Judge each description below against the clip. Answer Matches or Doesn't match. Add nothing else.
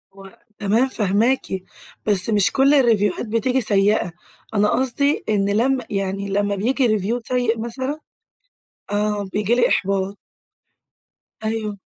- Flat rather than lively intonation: Doesn't match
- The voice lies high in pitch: Matches